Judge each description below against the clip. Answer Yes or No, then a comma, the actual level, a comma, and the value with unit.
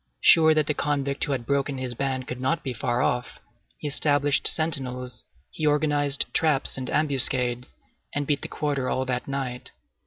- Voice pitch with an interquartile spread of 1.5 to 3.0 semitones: Yes, narrow, 2.4 semitones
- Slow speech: No, average, 175 wpm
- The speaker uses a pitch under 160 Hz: Yes, medium, 140 Hz